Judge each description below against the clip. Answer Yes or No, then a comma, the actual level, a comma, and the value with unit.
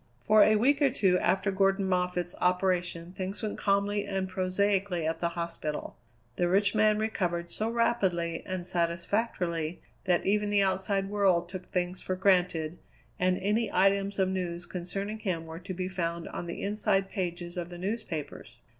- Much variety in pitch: No, narrow, 2.5 semitones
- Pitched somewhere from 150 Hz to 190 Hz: Yes, medium, 185 Hz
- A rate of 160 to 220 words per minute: Yes, average, 165 wpm